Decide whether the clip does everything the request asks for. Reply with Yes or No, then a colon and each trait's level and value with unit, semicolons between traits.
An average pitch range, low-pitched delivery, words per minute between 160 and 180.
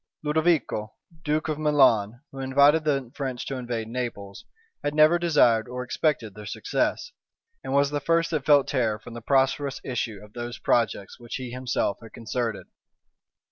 Yes: average, 4.3 semitones; low, 130 Hz; average, 165 wpm